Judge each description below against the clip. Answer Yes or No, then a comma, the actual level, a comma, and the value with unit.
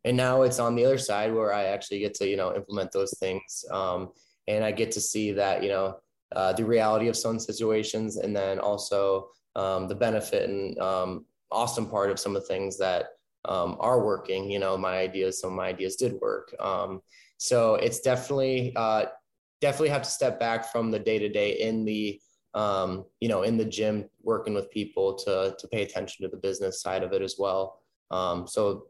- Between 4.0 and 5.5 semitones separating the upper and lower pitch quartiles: No, average, 3.4 semitones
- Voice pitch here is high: No, low, 105 Hz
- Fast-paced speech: Yes, fast, 210 wpm